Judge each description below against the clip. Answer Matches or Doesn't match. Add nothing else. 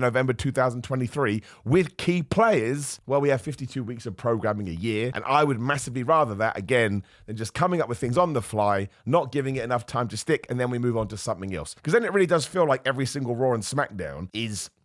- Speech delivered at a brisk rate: Matches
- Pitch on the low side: Matches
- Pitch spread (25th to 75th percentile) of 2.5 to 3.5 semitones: Doesn't match